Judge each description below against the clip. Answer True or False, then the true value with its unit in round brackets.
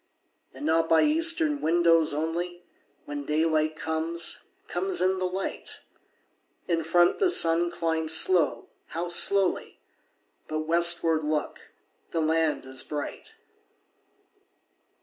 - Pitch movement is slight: True (1.9 semitones)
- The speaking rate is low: True (100 wpm)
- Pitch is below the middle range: False (165 Hz)